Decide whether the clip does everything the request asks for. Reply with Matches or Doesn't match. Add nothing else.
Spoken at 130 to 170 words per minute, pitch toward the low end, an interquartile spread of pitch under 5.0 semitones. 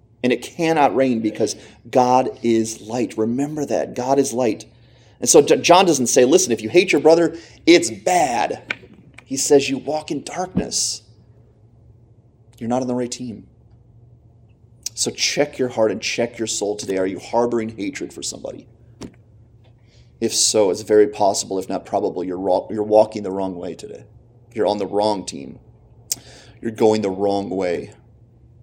Matches